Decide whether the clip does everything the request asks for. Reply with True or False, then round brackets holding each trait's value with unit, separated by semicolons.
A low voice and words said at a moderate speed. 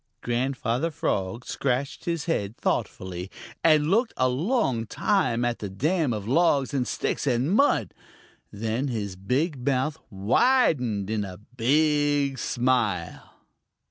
False (130 Hz; 125 wpm)